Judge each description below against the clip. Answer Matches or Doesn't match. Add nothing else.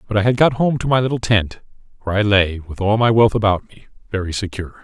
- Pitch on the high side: Doesn't match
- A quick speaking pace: Matches